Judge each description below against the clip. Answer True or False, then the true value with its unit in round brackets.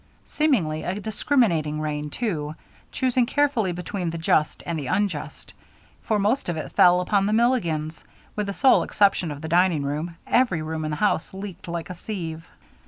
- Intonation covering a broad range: False (4.9 semitones)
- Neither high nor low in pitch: True (180 Hz)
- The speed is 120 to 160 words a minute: False (175 wpm)